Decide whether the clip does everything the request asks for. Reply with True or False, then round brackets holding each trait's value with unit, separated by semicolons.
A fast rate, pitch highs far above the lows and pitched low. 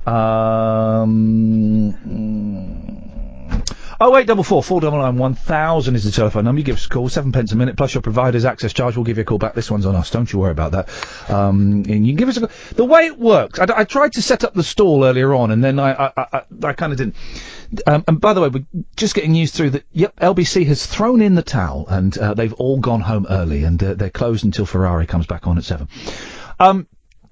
True (245 wpm; 7.5 semitones; 120 Hz)